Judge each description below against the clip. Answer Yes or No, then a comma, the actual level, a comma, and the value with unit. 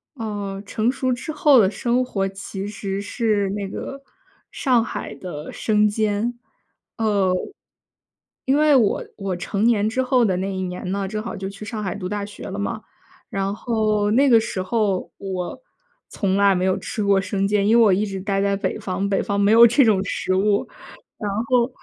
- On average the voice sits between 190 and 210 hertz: Yes, high, 205 Hz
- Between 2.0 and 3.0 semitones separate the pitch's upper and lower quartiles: Yes, narrow, 2.5 semitones